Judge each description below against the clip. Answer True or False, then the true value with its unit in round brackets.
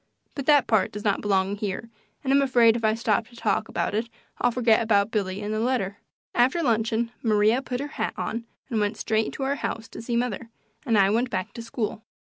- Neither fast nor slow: False (225 wpm)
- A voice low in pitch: False (225 Hz)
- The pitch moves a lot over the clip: False (2.6 semitones)